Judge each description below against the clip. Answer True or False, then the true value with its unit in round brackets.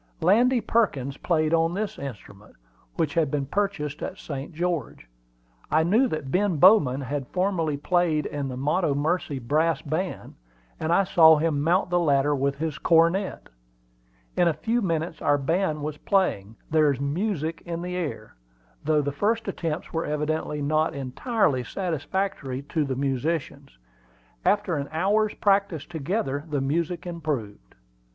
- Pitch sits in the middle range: True (160 Hz)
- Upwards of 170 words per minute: False (145 wpm)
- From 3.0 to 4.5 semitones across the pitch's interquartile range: True (4.1 semitones)